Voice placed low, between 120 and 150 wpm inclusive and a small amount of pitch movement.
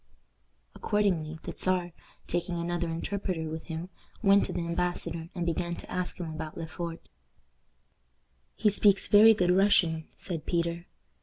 No: medium, 175 Hz; average, 145 wpm; narrow, 2.1 semitones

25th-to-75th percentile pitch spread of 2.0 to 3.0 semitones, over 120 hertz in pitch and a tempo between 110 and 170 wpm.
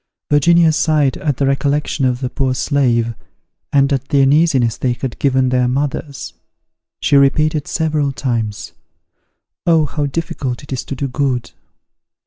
Yes: narrow, 2.6 semitones; medium, 140 Hz; average, 145 wpm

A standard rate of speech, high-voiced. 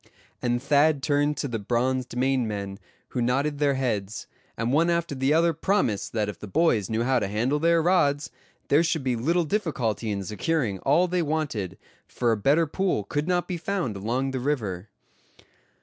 No: average, 185 wpm; low, 135 Hz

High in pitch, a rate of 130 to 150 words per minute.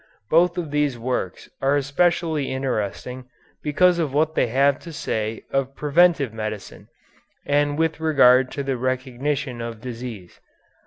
No: low, 135 Hz; average, 140 wpm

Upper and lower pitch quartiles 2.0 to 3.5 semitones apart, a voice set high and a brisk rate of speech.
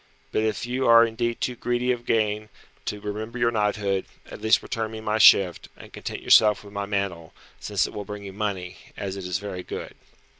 No: narrow, 2.4 semitones; low, 105 Hz; fast, 210 wpm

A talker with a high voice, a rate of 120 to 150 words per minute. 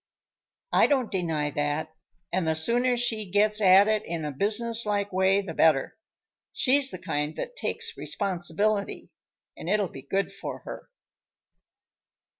Yes: high, 195 Hz; average, 140 wpm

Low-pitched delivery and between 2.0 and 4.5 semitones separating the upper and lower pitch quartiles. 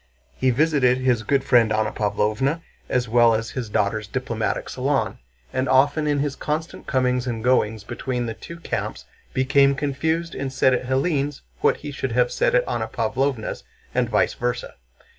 Yes: low, 130 Hz; average, 3.4 semitones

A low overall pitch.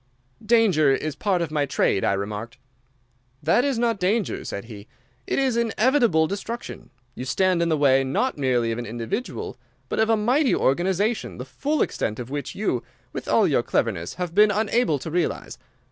No: medium, 170 Hz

